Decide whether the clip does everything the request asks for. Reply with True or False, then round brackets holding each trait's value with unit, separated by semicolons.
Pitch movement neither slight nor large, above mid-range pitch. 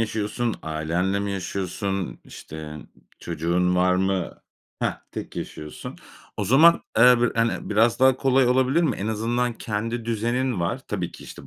False (5.0 semitones; 110 Hz)